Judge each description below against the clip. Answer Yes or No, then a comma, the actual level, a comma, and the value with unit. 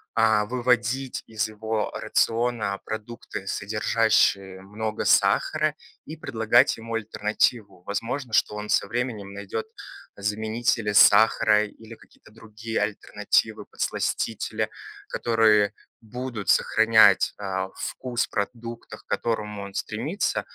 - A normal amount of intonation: No, narrow, 2.1 semitones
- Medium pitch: No, low, 110 Hz